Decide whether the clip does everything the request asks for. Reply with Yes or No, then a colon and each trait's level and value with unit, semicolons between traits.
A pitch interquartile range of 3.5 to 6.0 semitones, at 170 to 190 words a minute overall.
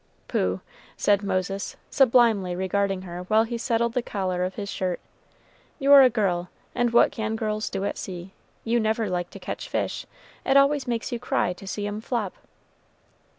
Yes: average, 4.0 semitones; average, 175 wpm